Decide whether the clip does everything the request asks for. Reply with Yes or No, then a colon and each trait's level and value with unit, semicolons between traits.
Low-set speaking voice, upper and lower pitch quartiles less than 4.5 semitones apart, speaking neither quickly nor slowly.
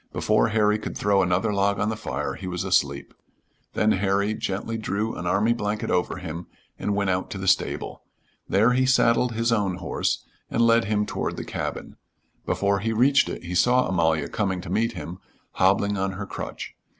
Yes: low, 100 Hz; average, 2.9 semitones; average, 190 wpm